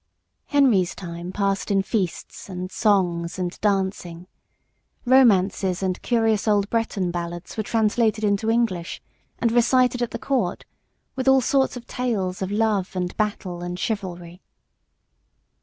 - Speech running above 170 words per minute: No, slow, 135 wpm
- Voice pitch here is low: No, high, 200 Hz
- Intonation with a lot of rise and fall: No, average, 3.9 semitones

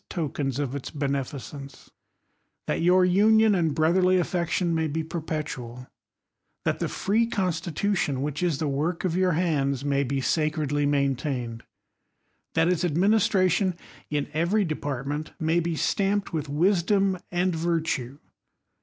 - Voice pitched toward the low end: No, medium, 160 Hz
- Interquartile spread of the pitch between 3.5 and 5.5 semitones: Yes, average, 4.3 semitones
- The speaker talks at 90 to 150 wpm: Yes, average, 145 wpm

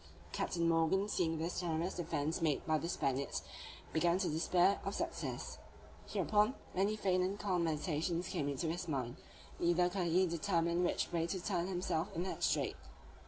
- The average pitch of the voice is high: No, medium, 170 Hz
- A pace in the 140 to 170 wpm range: Yes, average, 165 wpm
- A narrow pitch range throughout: Yes, narrow, 2.3 semitones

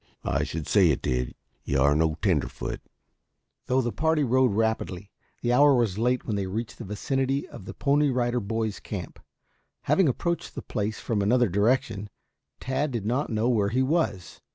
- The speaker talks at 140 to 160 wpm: No, average, 175 wpm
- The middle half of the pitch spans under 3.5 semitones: No, average, 4.8 semitones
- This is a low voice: Yes, low, 115 Hz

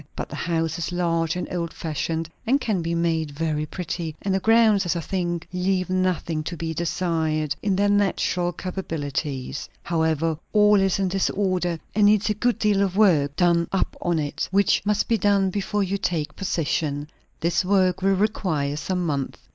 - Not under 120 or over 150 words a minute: No, average, 180 wpm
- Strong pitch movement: No, average, 3.2 semitones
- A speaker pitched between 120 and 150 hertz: No, medium, 175 Hz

